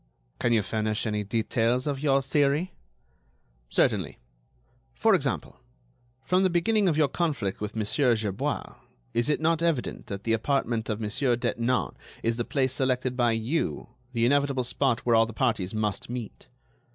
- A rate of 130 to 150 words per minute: No, average, 160 wpm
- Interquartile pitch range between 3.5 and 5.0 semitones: Yes, average, 4.1 semitones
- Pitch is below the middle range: Yes, low, 120 Hz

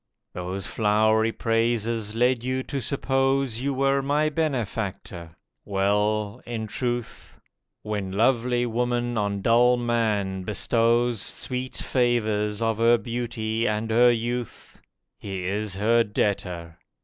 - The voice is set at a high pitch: No, low, 115 Hz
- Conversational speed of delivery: No, slow, 115 wpm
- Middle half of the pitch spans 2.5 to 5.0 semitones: Yes, average, 2.8 semitones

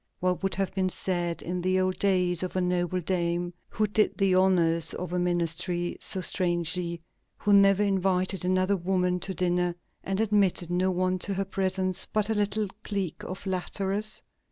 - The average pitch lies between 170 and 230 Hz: Yes, medium, 185 Hz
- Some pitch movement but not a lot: No, narrow, 1.6 semitones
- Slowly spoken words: No, average, 175 wpm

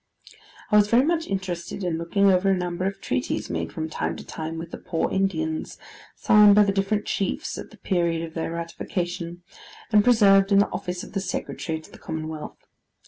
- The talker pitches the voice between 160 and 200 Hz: Yes, medium, 185 Hz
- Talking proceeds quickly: No, average, 195 wpm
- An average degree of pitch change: Yes, average, 3.1 semitones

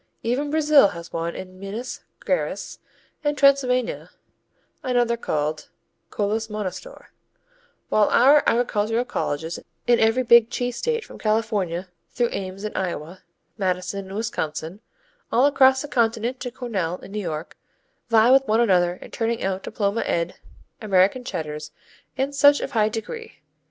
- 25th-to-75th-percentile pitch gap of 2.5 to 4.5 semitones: No, average, 5.1 semitones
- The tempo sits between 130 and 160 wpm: Yes, average, 140 wpm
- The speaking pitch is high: Yes, high, 220 Hz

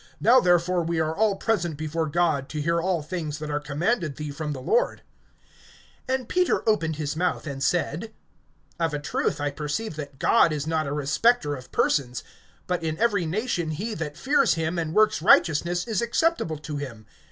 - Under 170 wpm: No, average, 185 wpm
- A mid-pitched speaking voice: Yes, medium, 160 Hz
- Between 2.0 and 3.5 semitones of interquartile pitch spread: No, average, 4.6 semitones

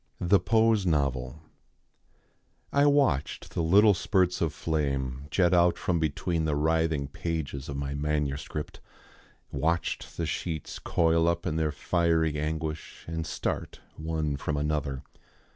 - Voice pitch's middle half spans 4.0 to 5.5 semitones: No, average, 2.7 semitones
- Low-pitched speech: Yes, very low, 80 Hz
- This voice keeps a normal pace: No, slow, 130 wpm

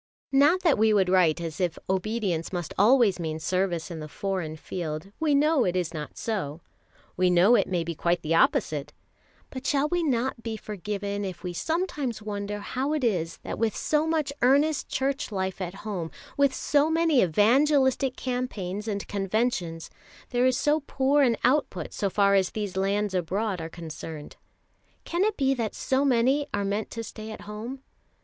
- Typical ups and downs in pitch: No, wide, 6.6 semitones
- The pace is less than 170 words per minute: No, average, 180 wpm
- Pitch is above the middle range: Yes, high, 210 Hz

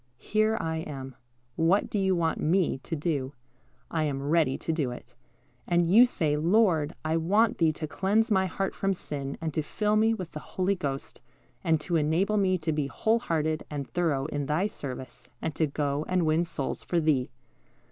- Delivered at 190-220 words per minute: Yes, average, 195 wpm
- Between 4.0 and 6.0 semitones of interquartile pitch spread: Yes, average, 4.3 semitones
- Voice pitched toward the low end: No, medium, 160 Hz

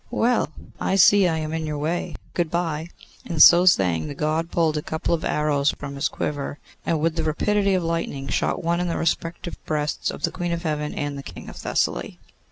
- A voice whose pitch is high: No, medium, 160 Hz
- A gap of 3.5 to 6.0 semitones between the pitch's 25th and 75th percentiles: No, narrow, 2.4 semitones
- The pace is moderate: No, fast, 215 wpm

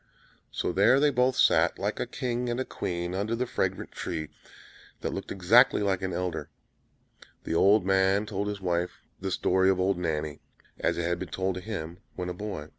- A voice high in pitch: No, very low, 95 Hz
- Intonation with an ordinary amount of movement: Yes, average, 3.1 semitones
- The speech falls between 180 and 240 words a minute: Yes, average, 190 wpm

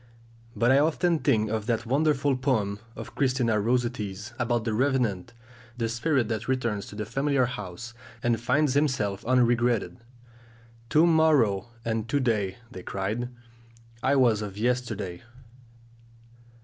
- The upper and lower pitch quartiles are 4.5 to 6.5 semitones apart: No, average, 3.6 semitones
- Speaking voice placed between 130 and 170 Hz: No, low, 120 Hz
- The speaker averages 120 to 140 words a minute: Yes, slow, 135 wpm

